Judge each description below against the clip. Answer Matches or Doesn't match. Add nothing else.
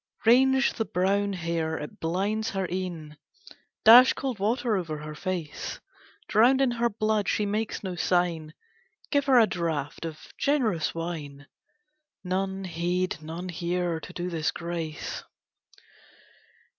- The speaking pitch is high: Doesn't match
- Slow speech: Matches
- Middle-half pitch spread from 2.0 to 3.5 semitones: Doesn't match